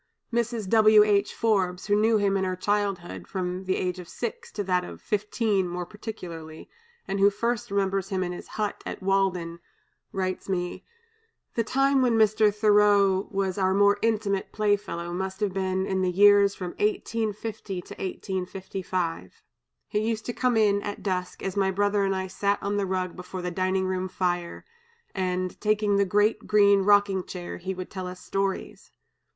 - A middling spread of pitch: No, narrow, 2.0 semitones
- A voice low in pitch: No, high, 195 Hz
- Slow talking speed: No, average, 175 wpm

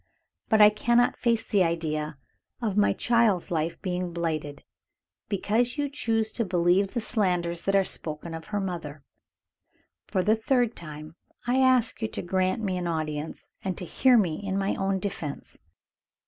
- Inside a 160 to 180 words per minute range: Yes, average, 165 wpm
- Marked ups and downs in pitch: No, average, 4.7 semitones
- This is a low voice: No, high, 190 Hz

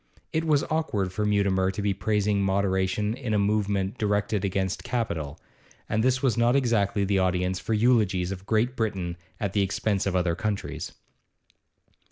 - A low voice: Yes, low, 100 Hz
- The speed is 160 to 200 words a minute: Yes, average, 165 wpm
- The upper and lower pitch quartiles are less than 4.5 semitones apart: Yes, narrow, 2.6 semitones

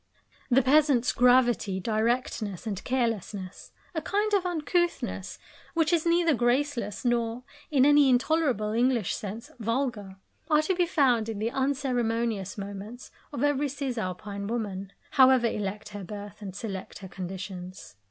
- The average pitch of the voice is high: Yes, high, 235 Hz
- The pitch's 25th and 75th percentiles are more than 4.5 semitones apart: Yes, average, 5.2 semitones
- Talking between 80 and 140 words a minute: Yes, slow, 135 wpm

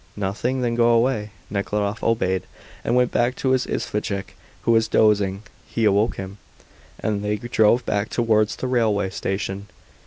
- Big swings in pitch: No, average, 2.8 semitones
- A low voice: Yes, low, 110 Hz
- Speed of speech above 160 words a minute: No, average, 155 wpm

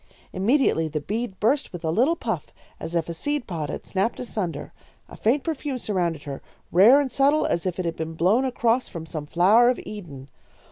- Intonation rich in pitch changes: Yes, wide, 7.2 semitones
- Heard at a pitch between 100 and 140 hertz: No, high, 195 Hz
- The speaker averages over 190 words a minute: Yes, average, 200 wpm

